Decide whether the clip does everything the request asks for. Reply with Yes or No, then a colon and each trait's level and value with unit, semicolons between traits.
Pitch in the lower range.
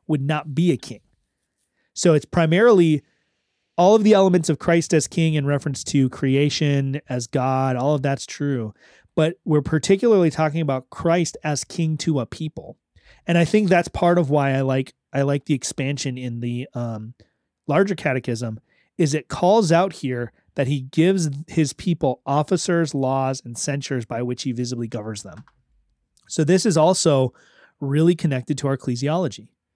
No: medium, 145 Hz